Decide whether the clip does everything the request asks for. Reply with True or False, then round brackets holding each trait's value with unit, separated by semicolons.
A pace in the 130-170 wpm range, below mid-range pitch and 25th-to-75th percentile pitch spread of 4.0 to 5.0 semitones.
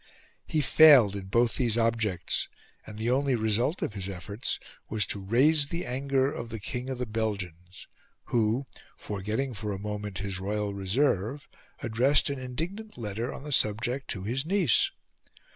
True (160 wpm; 115 Hz; 4.6 semitones)